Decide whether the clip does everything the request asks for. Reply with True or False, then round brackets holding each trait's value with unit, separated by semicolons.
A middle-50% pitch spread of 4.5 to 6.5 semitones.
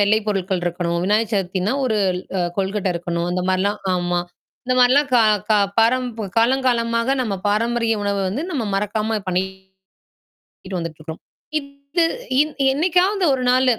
True (5.1 semitones)